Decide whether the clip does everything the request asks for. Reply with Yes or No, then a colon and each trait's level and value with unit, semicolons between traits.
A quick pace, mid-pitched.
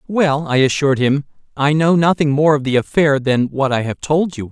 Yes: fast, 225 wpm; medium, 145 Hz